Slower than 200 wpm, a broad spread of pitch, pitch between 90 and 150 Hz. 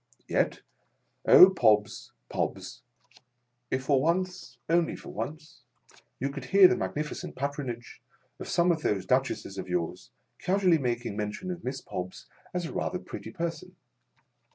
Yes: average, 155 wpm; wide, 6.4 semitones; medium, 140 Hz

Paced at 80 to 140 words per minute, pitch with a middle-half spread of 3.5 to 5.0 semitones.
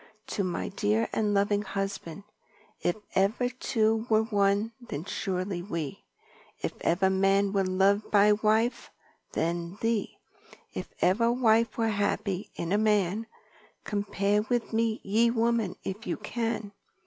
No: slow, 135 wpm; narrow, 2.5 semitones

